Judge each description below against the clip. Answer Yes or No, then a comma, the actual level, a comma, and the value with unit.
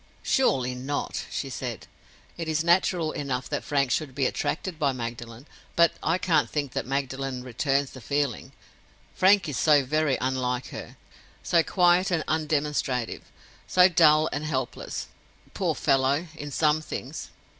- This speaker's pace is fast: No, average, 145 wpm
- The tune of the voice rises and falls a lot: No, average, 3.5 semitones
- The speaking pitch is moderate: Yes, medium, 145 Hz